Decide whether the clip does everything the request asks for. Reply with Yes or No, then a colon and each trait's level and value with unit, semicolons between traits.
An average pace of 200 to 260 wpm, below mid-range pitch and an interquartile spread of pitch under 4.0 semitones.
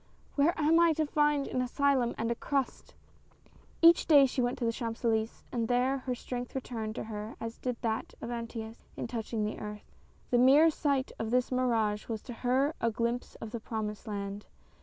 No: fast, 205 wpm; high, 240 Hz; average, 3.1 semitones